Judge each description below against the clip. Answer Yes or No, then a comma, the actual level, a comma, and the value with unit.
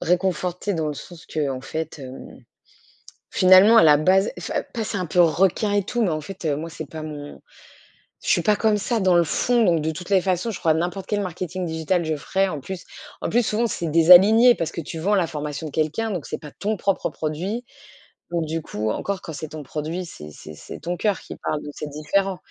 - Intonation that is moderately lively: Yes, average, 4.0 semitones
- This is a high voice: No, medium, 175 Hz